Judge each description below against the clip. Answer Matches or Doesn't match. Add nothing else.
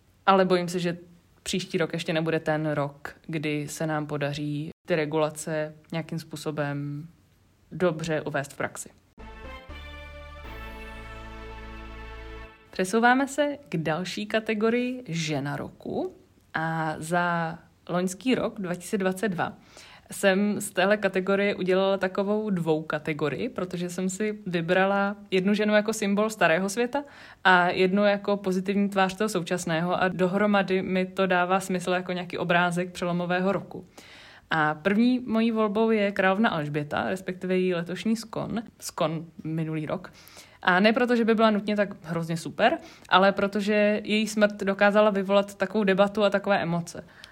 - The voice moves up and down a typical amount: Matches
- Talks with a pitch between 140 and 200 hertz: Matches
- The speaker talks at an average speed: Matches